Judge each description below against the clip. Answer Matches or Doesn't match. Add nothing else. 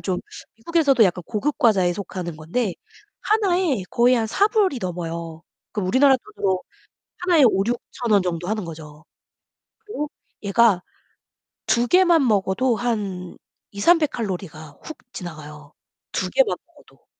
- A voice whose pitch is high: Matches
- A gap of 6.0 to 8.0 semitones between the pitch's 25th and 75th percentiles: Matches